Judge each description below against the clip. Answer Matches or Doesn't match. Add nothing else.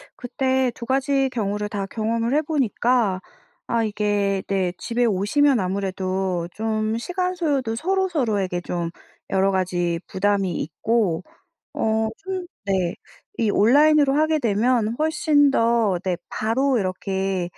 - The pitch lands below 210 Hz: Doesn't match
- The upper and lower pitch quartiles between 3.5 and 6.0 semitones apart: Matches